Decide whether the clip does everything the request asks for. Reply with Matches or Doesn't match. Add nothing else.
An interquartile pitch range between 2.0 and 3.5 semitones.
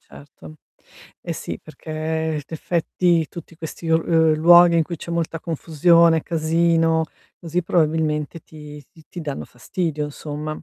Doesn't match